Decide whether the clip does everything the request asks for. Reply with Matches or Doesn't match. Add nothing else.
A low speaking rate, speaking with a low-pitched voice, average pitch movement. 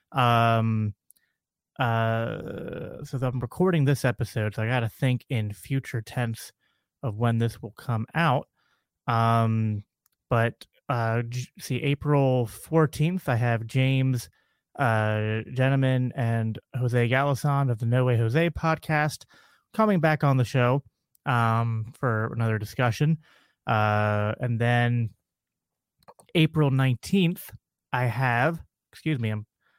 Matches